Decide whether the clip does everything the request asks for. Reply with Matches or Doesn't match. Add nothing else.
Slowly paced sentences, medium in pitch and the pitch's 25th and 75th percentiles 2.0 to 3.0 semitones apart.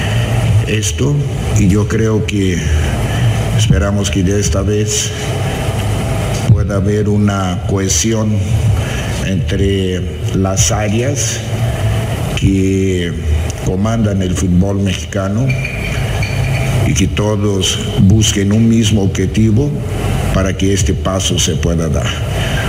Doesn't match